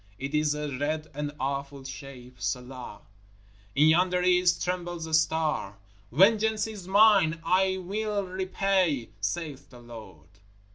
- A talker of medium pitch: Yes, medium, 160 Hz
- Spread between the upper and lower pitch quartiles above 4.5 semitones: Yes, average, 5.3 semitones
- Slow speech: Yes, slow, 130 wpm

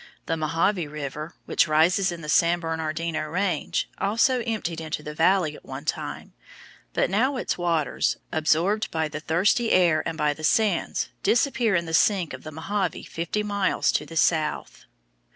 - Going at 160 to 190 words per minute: Yes, average, 170 wpm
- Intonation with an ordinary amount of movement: Yes, average, 4.0 semitones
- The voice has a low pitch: No, medium, 165 Hz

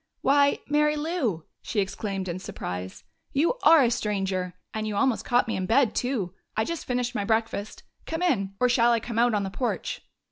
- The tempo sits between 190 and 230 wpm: Yes, average, 200 wpm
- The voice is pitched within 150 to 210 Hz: No, high, 230 Hz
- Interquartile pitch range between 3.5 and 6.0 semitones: Yes, wide, 5.5 semitones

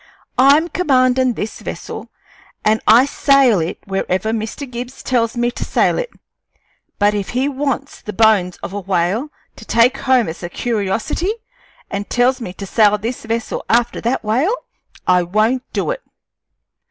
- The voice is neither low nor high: No, high, 230 Hz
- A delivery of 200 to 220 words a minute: No, average, 160 wpm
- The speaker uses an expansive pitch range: No, average, 4.0 semitones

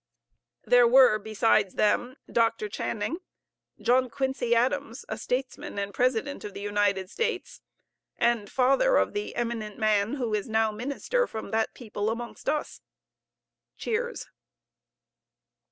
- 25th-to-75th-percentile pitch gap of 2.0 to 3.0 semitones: No, average, 3.8 semitones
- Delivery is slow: Yes, slow, 125 wpm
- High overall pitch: Yes, high, 235 Hz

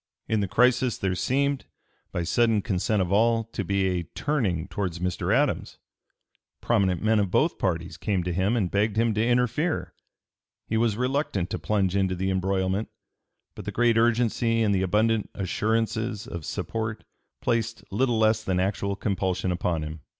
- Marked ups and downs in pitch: No, average, 3.5 semitones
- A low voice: Yes, low, 105 Hz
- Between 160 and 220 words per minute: Yes, average, 165 wpm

